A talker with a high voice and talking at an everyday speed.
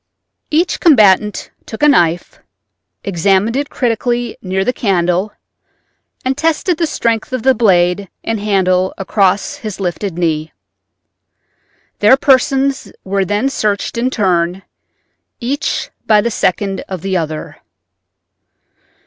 No: high, 205 Hz; slow, 120 wpm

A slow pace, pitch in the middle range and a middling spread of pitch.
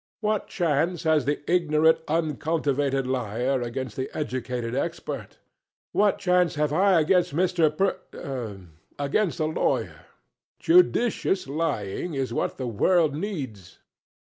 Yes: slow, 120 wpm; medium, 150 Hz; average, 4.9 semitones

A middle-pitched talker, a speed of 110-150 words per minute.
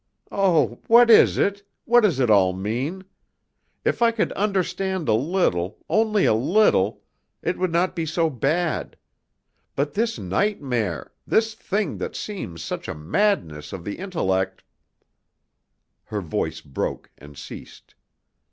Yes: medium, 160 Hz; average, 140 wpm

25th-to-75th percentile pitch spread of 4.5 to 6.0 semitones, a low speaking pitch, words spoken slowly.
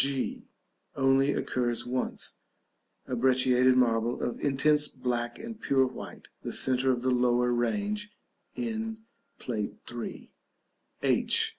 No: average, 3.3 semitones; low, 130 Hz; slow, 120 wpm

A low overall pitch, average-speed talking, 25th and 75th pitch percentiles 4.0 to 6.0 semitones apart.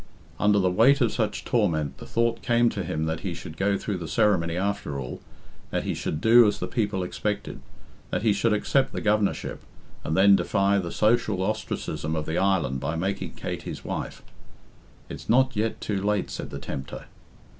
Yes: low, 100 Hz; average, 190 wpm; average, 4.5 semitones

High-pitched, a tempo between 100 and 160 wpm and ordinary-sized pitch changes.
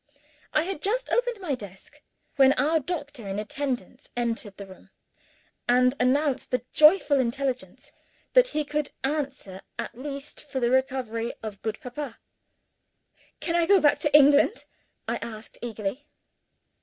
Yes: very high, 270 Hz; average, 145 wpm; average, 4.1 semitones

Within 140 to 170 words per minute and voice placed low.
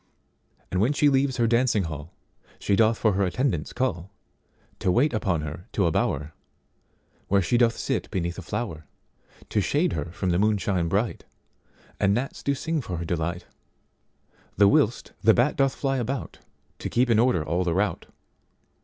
Yes: average, 155 wpm; low, 105 Hz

